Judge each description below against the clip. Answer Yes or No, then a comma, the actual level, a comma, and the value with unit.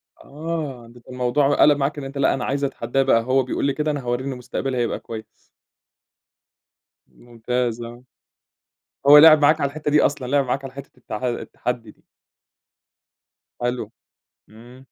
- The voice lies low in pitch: Yes, low, 130 Hz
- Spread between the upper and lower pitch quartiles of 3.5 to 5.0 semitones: No, average, 2.7 semitones